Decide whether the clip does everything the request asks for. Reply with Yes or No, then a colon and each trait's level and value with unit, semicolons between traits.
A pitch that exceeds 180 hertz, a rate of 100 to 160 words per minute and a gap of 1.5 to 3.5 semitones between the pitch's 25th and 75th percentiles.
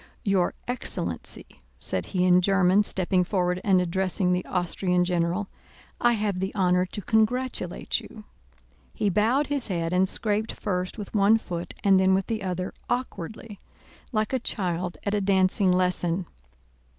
Yes: high, 190 Hz; average, 150 wpm; average, 2.7 semitones